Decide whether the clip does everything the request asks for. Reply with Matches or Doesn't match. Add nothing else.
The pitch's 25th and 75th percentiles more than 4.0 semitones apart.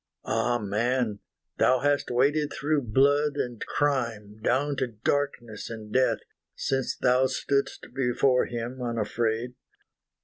Doesn't match